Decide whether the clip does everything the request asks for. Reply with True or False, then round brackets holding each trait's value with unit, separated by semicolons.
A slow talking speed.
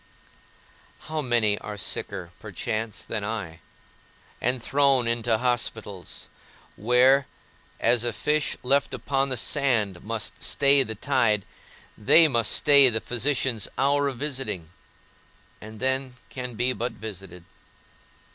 True (120 wpm)